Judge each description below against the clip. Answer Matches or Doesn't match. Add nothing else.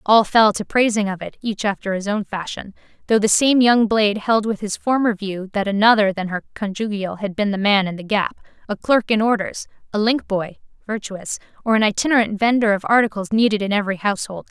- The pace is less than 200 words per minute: Doesn't match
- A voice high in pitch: Matches